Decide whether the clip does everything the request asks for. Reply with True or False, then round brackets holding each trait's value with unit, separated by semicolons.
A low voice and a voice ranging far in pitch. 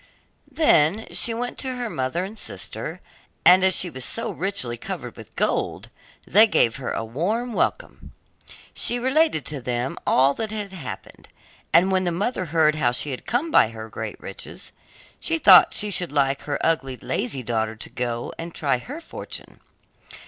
False (165 Hz; 8.6 semitones)